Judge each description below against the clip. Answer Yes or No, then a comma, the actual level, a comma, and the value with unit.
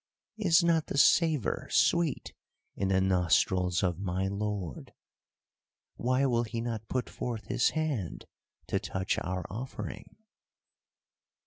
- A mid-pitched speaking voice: No, low, 110 Hz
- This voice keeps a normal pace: No, slow, 120 wpm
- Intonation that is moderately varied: No, wide, 6.3 semitones